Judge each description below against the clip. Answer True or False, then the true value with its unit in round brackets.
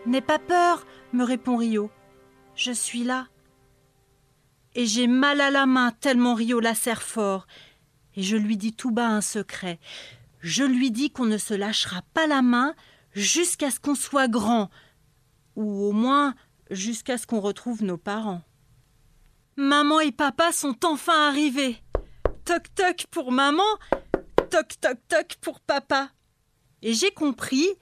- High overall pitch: True (240 Hz)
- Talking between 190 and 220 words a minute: False (150 wpm)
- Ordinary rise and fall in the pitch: False (7.8 semitones)